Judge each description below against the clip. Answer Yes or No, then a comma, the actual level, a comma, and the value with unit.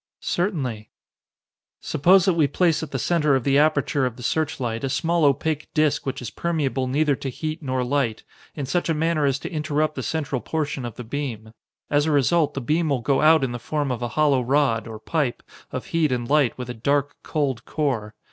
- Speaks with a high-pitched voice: No, medium, 140 Hz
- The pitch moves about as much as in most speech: Yes, average, 3.5 semitones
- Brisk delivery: Yes, fast, 215 wpm